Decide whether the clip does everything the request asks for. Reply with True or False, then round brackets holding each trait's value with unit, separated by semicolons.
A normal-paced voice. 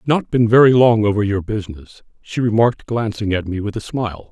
False (225 wpm)